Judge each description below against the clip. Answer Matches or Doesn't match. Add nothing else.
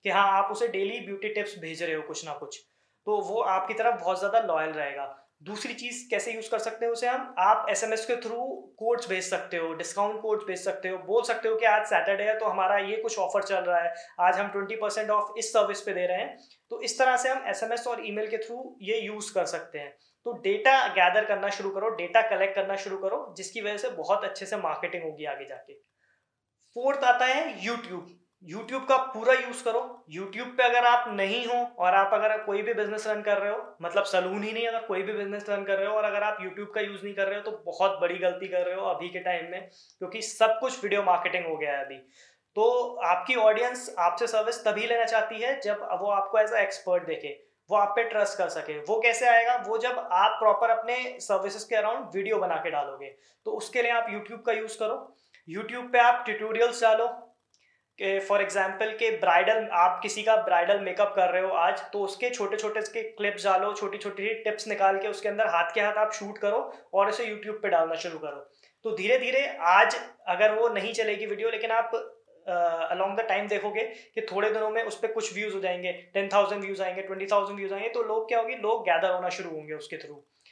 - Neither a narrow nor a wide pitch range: Matches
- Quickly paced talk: Matches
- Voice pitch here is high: Matches